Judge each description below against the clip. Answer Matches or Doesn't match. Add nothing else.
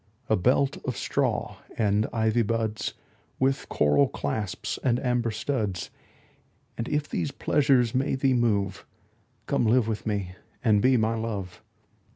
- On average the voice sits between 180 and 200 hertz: Doesn't match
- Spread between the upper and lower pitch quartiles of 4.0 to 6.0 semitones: Doesn't match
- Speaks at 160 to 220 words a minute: Doesn't match